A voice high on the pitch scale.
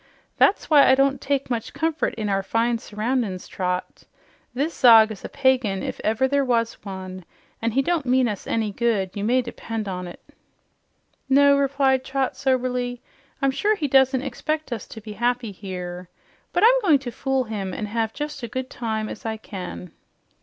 Yes: high, 240 Hz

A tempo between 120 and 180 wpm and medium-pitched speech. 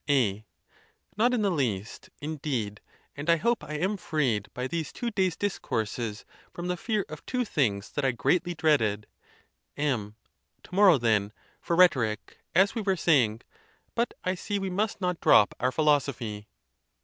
Yes: average, 160 wpm; medium, 150 Hz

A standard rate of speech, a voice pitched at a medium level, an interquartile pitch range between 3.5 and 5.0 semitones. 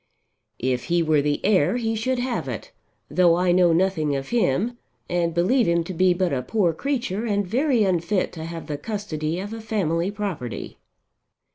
Yes: average, 180 wpm; medium, 180 Hz; average, 4.7 semitones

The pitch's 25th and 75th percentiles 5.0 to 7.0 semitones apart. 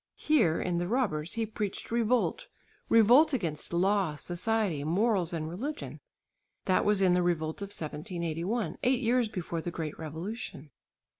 Yes: wide, 5.4 semitones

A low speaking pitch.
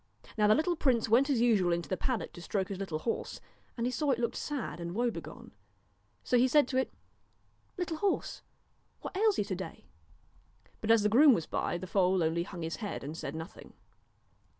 No: high, 220 Hz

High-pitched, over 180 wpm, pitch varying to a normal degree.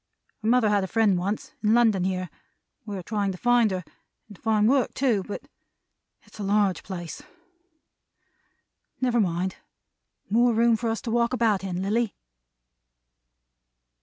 No: high, 210 Hz; average, 155 wpm; average, 3.5 semitones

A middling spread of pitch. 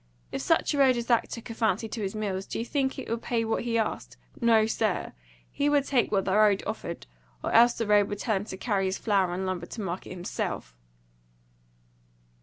Yes: average, 3.5 semitones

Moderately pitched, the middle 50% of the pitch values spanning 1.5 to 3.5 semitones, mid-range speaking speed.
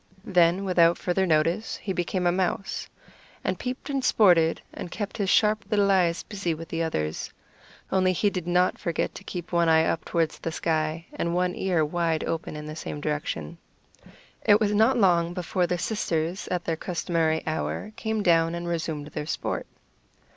Yes: medium, 175 Hz; average, 2.8 semitones; average, 180 wpm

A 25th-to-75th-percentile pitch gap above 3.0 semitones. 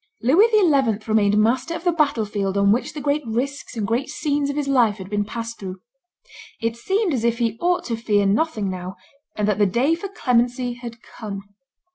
Yes: average, 5.3 semitones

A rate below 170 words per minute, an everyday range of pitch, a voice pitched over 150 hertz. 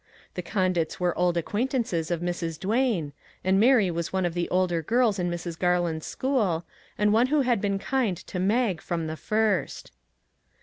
No: average, 175 wpm; average, 4.3 semitones; medium, 185 Hz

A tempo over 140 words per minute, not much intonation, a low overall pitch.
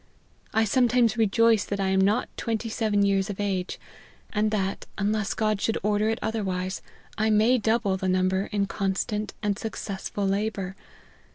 No: average, 170 wpm; narrow, 2.2 semitones; high, 205 Hz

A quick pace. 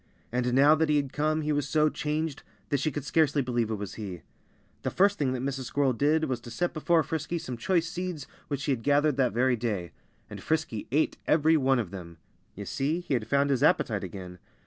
Yes: fast, 225 wpm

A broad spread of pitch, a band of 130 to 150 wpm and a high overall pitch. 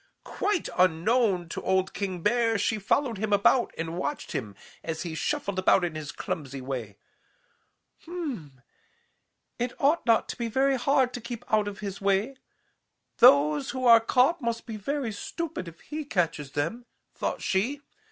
No: wide, 6.9 semitones; average, 165 wpm; high, 210 Hz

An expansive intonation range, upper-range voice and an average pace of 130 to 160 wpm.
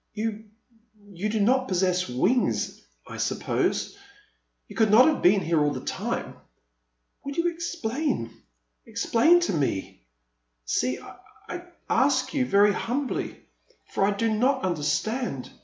Yes: wide, 6.4 semitones; high, 220 Hz; average, 140 wpm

